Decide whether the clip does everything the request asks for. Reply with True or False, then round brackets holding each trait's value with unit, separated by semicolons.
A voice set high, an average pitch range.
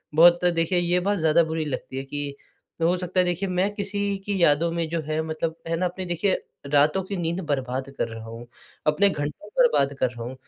False (165 Hz; 3.8 semitones)